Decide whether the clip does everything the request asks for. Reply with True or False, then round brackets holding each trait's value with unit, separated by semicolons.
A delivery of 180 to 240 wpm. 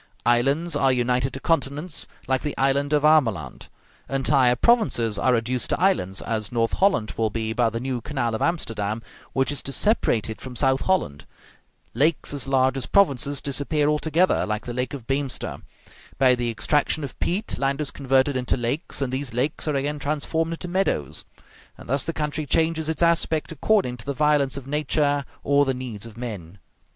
True (185 wpm)